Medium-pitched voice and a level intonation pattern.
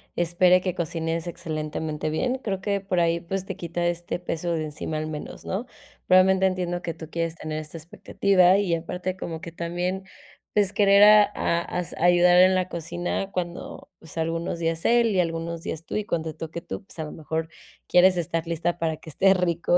Yes: medium, 175 Hz; narrow, 2.1 semitones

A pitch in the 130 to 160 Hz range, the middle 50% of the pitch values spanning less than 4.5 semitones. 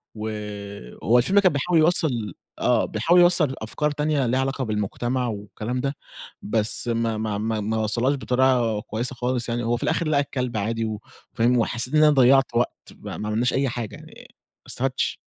No: low, 120 Hz; average, 3.6 semitones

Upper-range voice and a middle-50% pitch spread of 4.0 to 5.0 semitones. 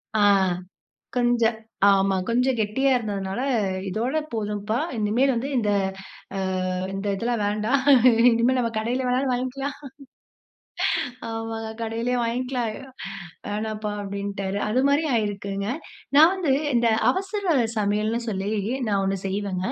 No: high, 225 Hz; average, 3.4 semitones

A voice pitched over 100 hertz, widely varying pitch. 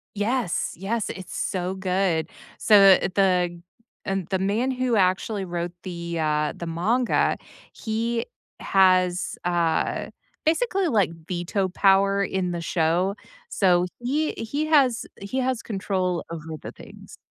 No: high, 190 Hz; average, 4.3 semitones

